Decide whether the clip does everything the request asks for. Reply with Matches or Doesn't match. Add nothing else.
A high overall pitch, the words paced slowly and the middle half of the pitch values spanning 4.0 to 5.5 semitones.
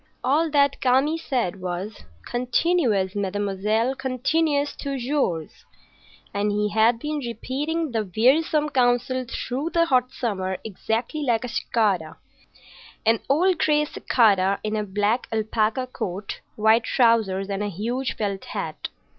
Matches